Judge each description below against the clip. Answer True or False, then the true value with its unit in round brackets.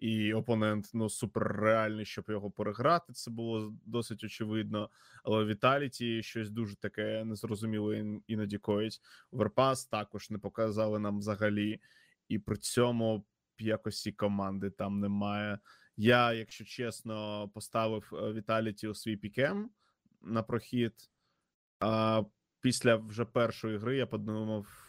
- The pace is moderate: True (125 wpm)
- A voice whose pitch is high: False (110 Hz)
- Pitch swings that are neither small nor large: False (1.4 semitones)